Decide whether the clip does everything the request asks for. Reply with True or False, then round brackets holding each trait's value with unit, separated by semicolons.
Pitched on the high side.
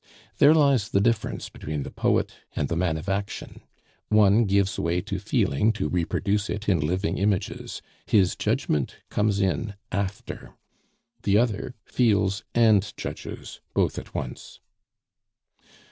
False (100 Hz)